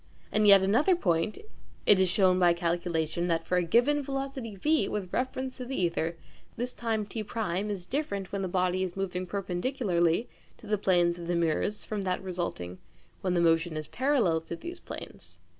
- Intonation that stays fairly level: No, average, 4.6 semitones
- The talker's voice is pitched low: No, high, 190 Hz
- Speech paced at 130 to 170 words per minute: No, average, 185 wpm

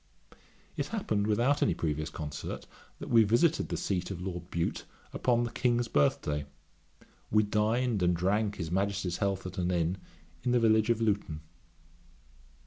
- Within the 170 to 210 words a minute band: No, average, 155 wpm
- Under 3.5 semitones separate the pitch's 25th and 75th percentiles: No, average, 4.6 semitones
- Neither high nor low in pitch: No, low, 100 Hz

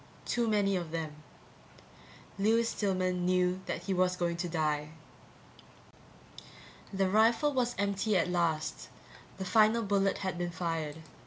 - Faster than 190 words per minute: No, slow, 135 wpm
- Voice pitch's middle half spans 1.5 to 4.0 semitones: Yes, average, 3.1 semitones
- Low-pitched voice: No, medium, 185 Hz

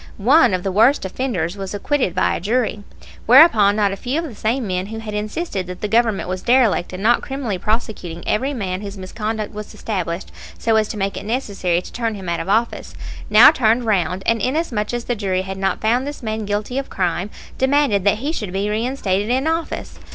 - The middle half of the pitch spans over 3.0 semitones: Yes, average, 4.0 semitones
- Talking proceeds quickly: Yes, fast, 215 wpm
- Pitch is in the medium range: No, high, 215 Hz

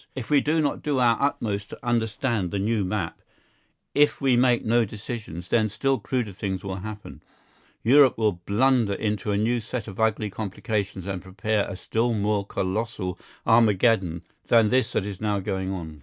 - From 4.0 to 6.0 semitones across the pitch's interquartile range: No, average, 3.4 semitones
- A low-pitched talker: Yes, low, 110 Hz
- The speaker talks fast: No, average, 175 wpm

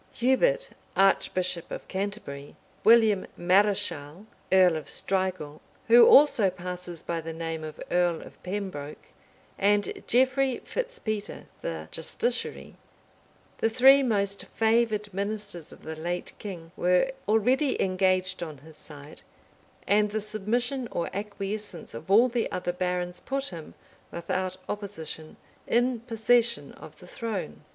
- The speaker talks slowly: Yes, slow, 130 wpm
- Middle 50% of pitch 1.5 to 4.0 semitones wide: No, average, 4.4 semitones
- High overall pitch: Yes, high, 195 Hz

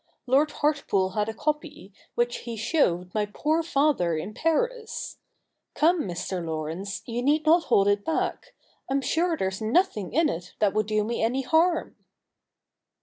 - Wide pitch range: Yes, wide, 7.7 semitones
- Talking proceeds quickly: No, average, 155 wpm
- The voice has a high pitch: Yes, high, 240 Hz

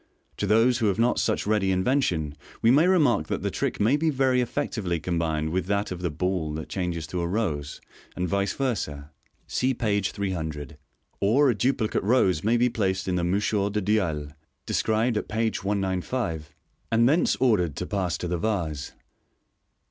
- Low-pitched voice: Yes, low, 100 Hz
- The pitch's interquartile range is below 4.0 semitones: No, average, 4.9 semitones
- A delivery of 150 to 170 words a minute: No, average, 180 wpm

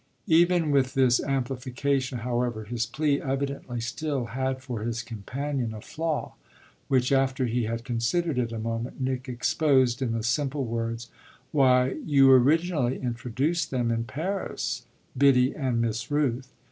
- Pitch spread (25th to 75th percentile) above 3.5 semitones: No, average, 2.7 semitones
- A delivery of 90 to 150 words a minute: Yes, average, 145 wpm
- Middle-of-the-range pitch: No, low, 130 Hz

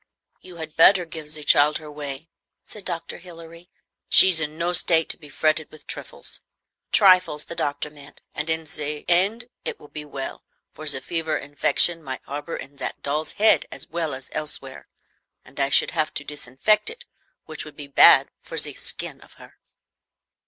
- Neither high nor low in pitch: Yes, medium, 155 Hz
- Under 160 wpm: No, average, 180 wpm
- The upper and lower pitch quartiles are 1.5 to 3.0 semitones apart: Yes, narrow, 2.6 semitones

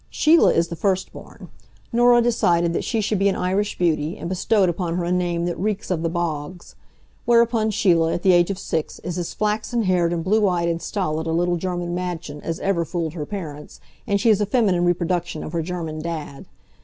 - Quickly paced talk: Yes, fast, 215 wpm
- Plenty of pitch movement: No, average, 3.0 semitones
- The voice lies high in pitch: No, medium, 175 Hz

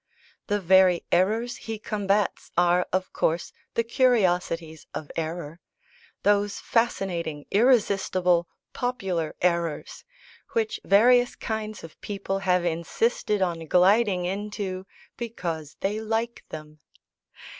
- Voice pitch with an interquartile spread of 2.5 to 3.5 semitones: No, average, 3.9 semitones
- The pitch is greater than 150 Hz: Yes, high, 190 Hz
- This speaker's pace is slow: Yes, slow, 105 wpm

